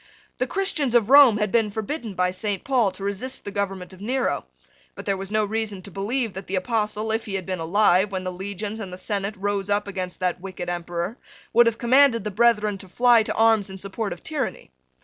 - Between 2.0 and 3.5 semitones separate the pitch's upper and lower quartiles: Yes, average, 3.0 semitones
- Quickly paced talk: Yes, fast, 225 wpm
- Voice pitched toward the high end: Yes, high, 205 Hz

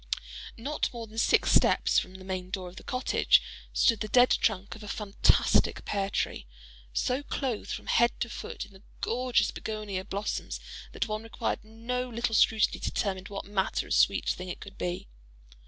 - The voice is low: No, high, 215 Hz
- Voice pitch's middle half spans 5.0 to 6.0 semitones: No, average, 3.3 semitones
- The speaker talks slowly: No, average, 185 wpm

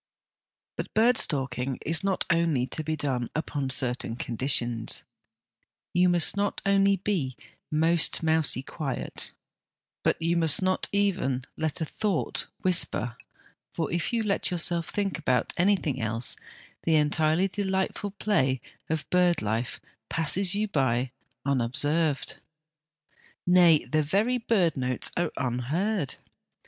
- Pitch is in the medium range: Yes, medium, 160 Hz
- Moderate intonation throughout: No, wide, 5.8 semitones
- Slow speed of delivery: Yes, slow, 125 wpm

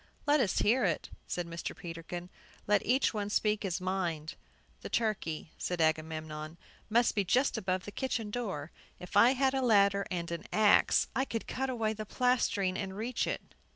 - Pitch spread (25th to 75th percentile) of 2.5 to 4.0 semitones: No, average, 5.1 semitones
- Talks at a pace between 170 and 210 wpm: Yes, average, 180 wpm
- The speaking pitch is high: Yes, high, 200 Hz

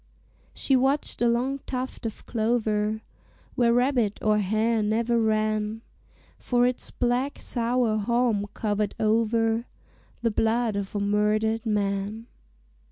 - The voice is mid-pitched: No, high, 225 Hz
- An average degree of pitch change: No, narrow, 2.2 semitones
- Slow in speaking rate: Yes, slow, 120 wpm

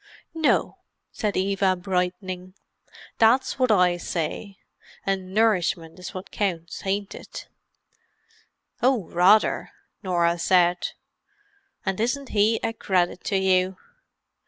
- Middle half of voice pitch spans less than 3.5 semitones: Yes, average, 2.9 semitones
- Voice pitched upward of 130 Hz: Yes, high, 190 Hz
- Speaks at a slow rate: Yes, slow, 110 wpm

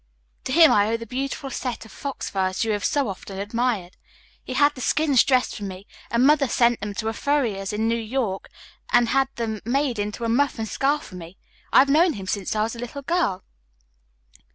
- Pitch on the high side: Yes, high, 230 Hz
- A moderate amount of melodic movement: Yes, average, 4.8 semitones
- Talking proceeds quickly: Yes, fast, 220 wpm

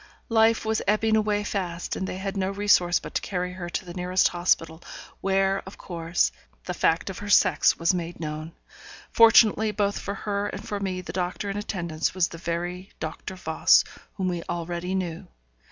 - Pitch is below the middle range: No, medium, 185 Hz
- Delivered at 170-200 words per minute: Yes, average, 185 wpm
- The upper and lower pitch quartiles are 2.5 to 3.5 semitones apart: Yes, average, 2.8 semitones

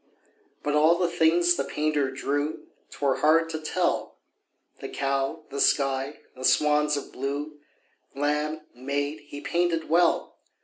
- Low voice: No, medium, 150 Hz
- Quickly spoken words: No, slow, 135 wpm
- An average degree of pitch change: No, narrow, 2.3 semitones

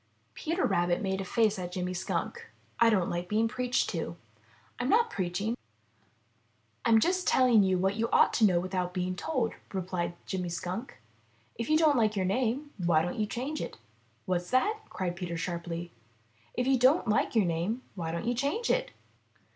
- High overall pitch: Yes, high, 205 Hz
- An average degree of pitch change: No, wide, 5.8 semitones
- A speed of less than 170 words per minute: No, average, 185 wpm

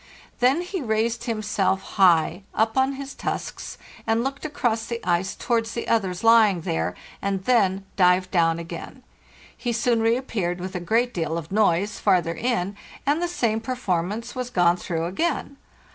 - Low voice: No, high, 215 Hz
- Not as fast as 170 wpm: Yes, average, 160 wpm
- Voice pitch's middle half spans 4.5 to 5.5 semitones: Yes, average, 4.9 semitones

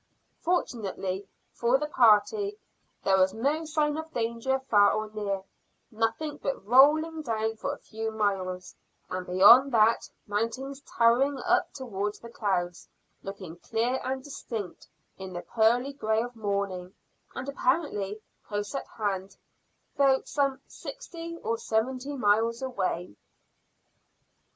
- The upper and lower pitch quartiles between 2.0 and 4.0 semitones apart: No, average, 5.1 semitones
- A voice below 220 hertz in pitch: No, high, 230 Hz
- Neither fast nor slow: No, slow, 125 wpm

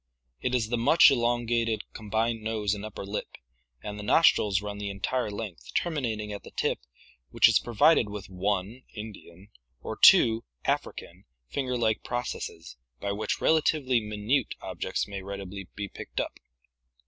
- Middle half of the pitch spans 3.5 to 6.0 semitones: No, average, 2.9 semitones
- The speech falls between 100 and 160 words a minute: Yes, average, 150 wpm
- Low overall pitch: Yes, low, 110 Hz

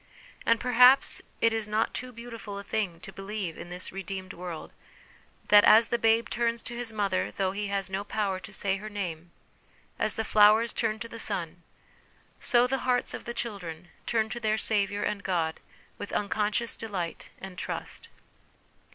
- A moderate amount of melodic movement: Yes, average, 3.1 semitones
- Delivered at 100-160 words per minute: No, average, 175 wpm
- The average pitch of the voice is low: No, high, 210 Hz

